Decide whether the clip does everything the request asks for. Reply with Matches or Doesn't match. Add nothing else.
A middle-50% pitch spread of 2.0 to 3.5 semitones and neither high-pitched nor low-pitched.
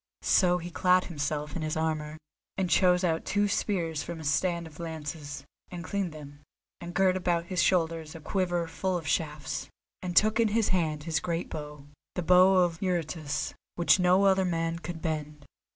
Matches